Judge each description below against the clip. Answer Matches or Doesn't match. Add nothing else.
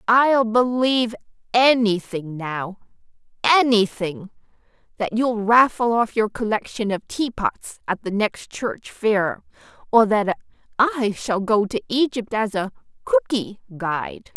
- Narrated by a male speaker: Doesn't match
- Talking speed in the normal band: Doesn't match